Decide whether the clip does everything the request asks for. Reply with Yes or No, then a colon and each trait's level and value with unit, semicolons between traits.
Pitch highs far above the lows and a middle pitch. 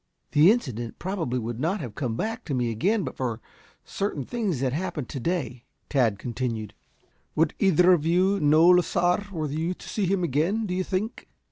Yes: wide, 6.7 semitones; medium, 160 Hz